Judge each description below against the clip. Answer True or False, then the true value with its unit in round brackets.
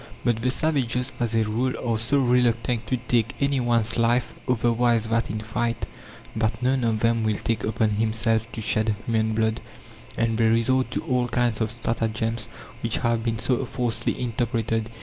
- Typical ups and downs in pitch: False (1.6 semitones)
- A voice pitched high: False (115 Hz)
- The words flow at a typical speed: True (175 wpm)